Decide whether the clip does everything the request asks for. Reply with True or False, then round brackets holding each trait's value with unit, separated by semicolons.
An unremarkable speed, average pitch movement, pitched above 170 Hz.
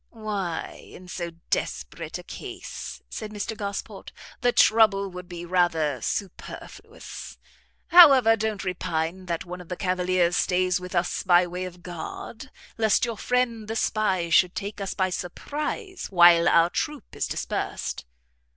True (145 wpm; 3.6 semitones; 185 Hz)